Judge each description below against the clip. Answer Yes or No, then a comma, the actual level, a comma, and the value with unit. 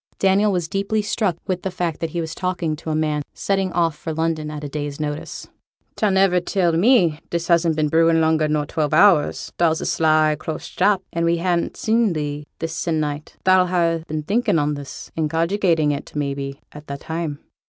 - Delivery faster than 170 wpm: Yes, average, 200 wpm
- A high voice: No, medium, 165 Hz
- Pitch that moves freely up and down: No, average, 3.0 semitones